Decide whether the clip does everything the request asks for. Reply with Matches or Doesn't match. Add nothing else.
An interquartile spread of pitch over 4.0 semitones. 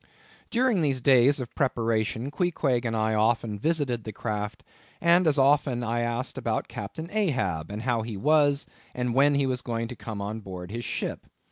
Matches